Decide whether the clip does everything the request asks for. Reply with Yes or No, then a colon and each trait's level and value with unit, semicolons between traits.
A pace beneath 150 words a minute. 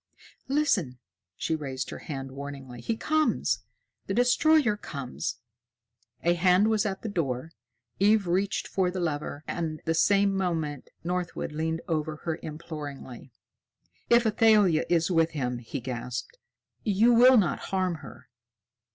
Yes: slow, 135 wpm